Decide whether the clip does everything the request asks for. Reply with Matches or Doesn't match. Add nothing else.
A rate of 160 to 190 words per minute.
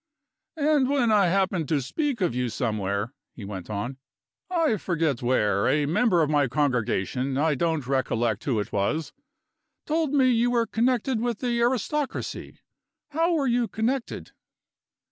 Doesn't match